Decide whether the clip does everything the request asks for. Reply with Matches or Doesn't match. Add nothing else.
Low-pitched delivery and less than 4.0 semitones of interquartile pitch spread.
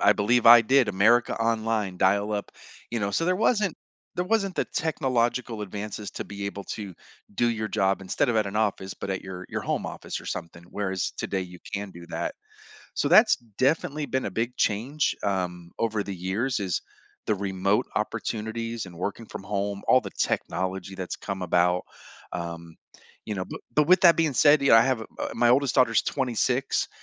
Doesn't match